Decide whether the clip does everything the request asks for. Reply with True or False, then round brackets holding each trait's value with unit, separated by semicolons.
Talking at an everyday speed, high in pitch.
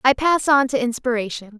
True (190 wpm; 250 Hz)